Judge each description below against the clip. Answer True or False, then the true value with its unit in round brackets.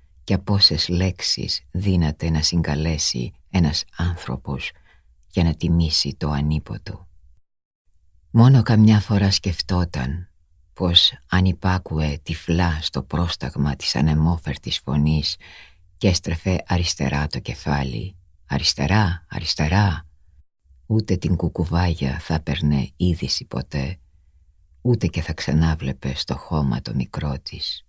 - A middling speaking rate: False (110 wpm)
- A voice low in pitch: True (80 Hz)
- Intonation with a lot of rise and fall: False (3.4 semitones)